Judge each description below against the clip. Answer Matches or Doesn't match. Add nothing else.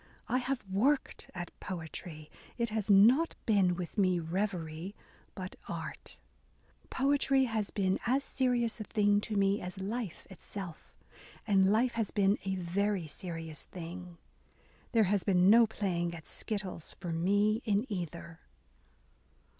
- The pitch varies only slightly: Doesn't match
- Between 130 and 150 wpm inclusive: Matches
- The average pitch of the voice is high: Matches